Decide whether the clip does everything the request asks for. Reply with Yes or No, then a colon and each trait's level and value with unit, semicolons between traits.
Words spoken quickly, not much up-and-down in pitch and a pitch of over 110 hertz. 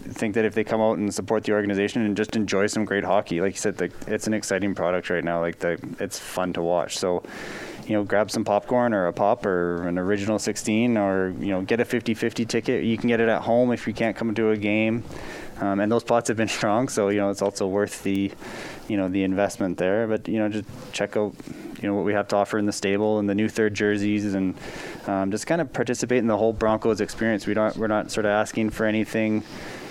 No: fast, 245 wpm; narrow, 1.9 semitones; low, 105 Hz